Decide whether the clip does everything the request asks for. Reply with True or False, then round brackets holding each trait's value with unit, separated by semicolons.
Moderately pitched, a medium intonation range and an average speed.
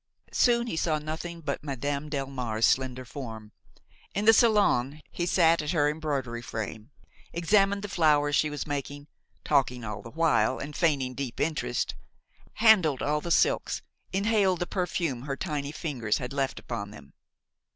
True (145 Hz; 4.8 semitones; 150 wpm)